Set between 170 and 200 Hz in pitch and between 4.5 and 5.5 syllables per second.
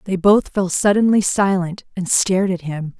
Yes: high, 190 Hz; 4.7 syllables/s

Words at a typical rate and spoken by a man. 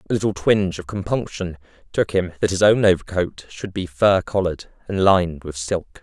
Yes: average, 190 wpm; male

